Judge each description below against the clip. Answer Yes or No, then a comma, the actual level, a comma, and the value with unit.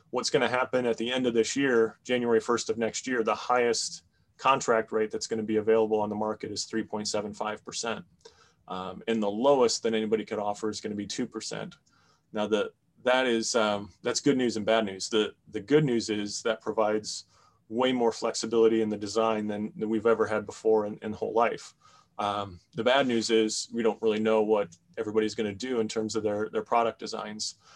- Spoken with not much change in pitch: Yes, narrow, 1.5 semitones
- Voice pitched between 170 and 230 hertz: No, low, 110 Hz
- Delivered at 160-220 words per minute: Yes, average, 200 wpm